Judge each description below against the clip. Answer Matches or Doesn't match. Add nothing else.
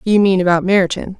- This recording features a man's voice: Doesn't match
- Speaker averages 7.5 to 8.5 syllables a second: Doesn't match